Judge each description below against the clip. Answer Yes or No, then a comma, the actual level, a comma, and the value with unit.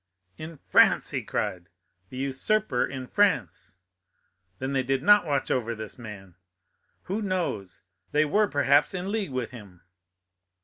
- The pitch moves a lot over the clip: Yes, wide, 7.7 semitones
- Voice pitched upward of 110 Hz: Yes, low, 135 Hz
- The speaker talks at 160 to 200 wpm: No, average, 140 wpm